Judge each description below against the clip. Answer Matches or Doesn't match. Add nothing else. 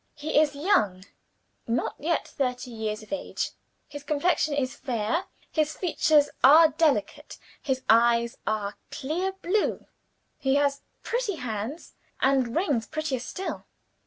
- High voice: Matches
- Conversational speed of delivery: Doesn't match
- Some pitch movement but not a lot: Matches